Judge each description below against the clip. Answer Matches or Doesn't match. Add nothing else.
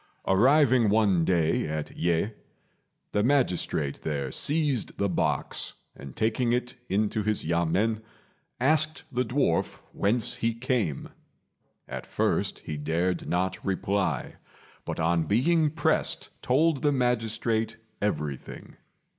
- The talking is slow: Matches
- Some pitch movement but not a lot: Doesn't match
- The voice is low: Matches